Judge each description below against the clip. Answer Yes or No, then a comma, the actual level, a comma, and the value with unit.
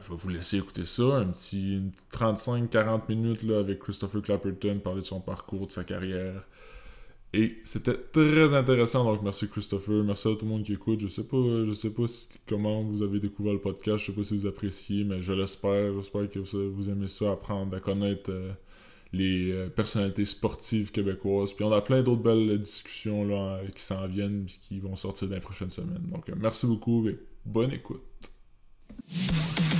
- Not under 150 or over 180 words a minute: No, average, 205 wpm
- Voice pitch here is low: Yes, low, 100 Hz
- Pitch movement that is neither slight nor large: No, narrow, 2.3 semitones